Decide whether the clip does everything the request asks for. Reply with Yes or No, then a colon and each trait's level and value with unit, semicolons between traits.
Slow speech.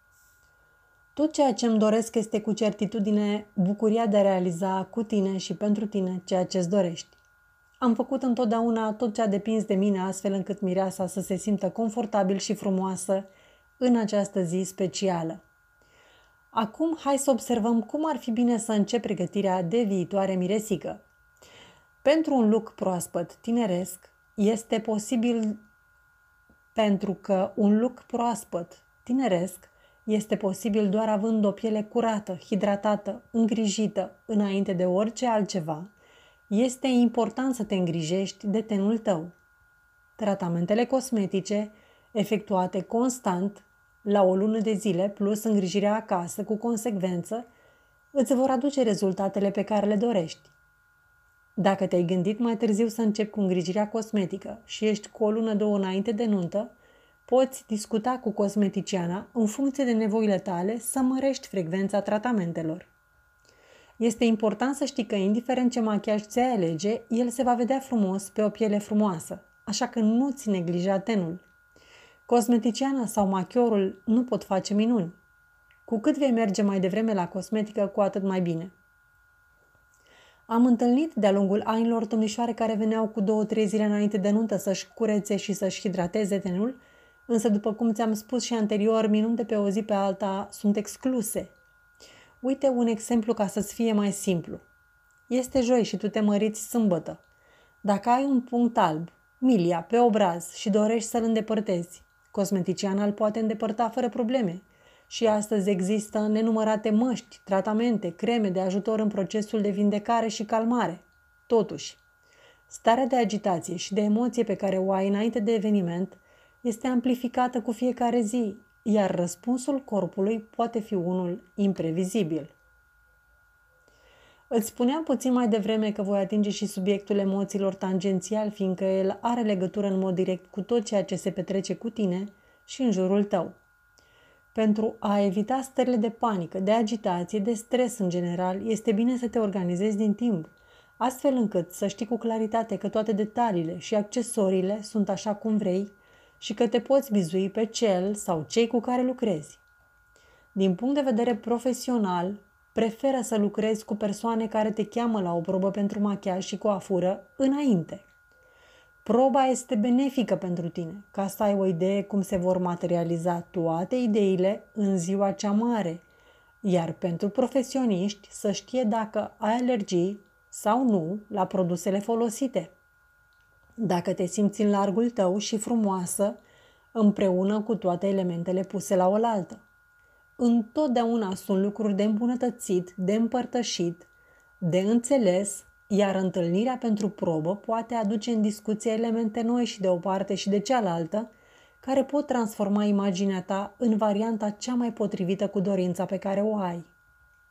No: average, 145 wpm